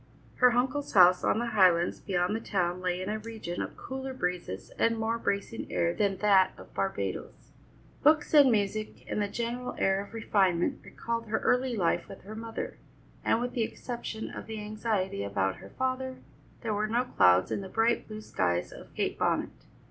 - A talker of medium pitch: No, high, 215 Hz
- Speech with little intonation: No, average, 4.0 semitones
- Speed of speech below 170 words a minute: No, average, 185 wpm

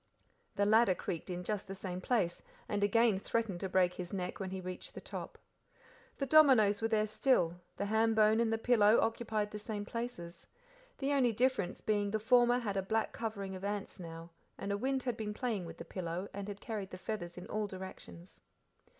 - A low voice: No, high, 205 Hz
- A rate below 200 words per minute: No, fast, 205 wpm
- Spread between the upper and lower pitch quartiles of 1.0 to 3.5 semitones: Yes, average, 3.1 semitones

